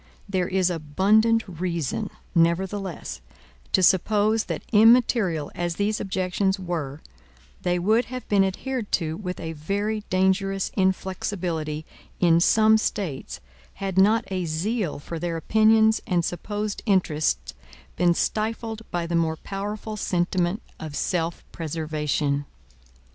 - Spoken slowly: Yes, slow, 120 wpm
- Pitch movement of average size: Yes, average, 3.9 semitones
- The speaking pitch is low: No, medium, 185 Hz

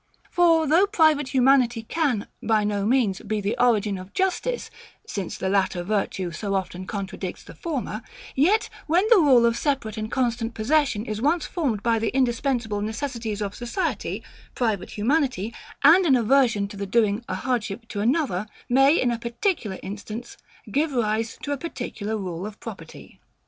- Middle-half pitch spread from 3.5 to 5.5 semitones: Yes, average, 5.1 semitones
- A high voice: Yes, high, 235 Hz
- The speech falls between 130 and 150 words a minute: No, average, 165 wpm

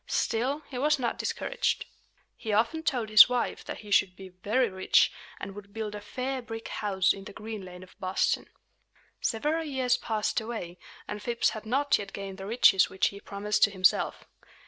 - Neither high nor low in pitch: No, high, 215 Hz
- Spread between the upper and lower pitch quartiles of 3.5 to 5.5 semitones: Yes, average, 4.0 semitones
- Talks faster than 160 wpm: Yes, average, 190 wpm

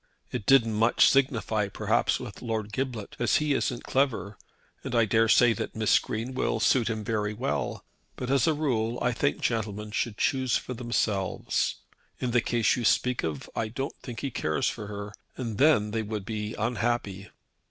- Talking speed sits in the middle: Yes, average, 180 wpm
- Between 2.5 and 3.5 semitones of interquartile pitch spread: Yes, average, 2.9 semitones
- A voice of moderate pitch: No, low, 115 Hz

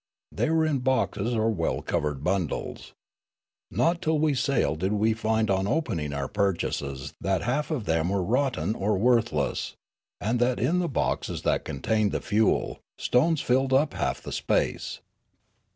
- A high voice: No, low, 110 Hz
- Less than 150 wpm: No, average, 160 wpm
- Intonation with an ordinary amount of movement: No, wide, 5.7 semitones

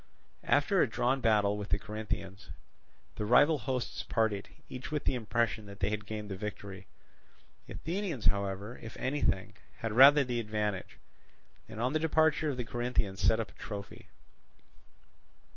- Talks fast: No, average, 160 wpm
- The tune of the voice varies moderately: Yes, average, 3.8 semitones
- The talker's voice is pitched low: Yes, low, 110 Hz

